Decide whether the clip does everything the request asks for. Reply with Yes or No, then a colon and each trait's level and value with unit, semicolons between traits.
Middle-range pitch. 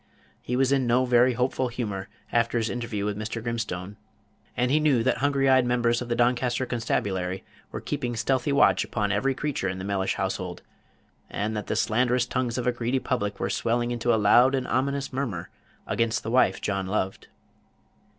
No: low, 120 Hz